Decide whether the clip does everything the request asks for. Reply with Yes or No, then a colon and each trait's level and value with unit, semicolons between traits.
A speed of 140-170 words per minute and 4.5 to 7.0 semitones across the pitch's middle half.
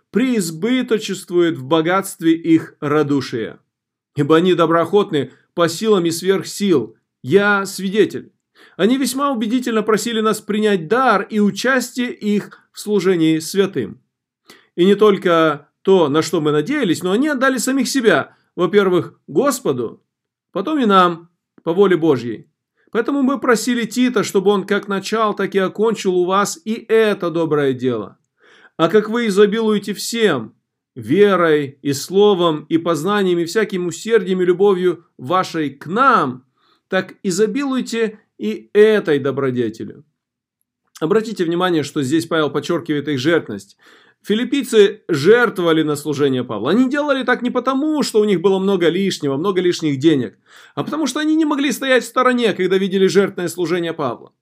Yes: average, 145 wpm; average, 5.1 semitones